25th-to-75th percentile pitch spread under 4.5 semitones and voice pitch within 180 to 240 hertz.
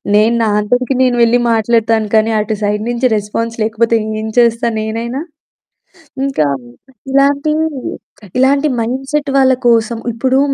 Yes: average, 2.9 semitones; high, 235 Hz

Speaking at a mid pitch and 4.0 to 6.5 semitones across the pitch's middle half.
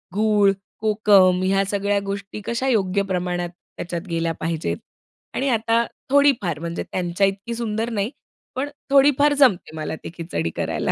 No: high, 200 Hz; average, 4.7 semitones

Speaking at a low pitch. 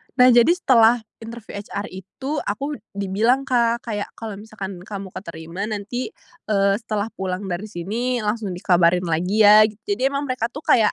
No: high, 210 Hz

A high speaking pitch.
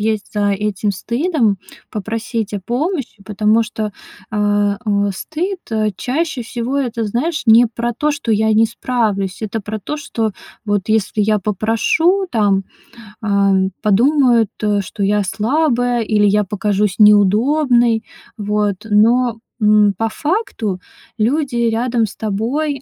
Yes: high, 220 Hz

